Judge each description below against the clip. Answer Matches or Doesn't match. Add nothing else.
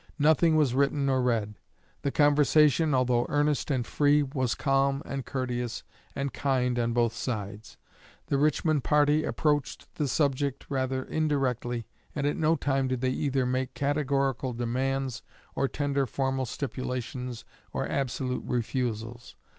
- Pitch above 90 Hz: Matches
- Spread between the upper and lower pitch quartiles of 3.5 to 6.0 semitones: Doesn't match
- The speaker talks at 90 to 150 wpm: Matches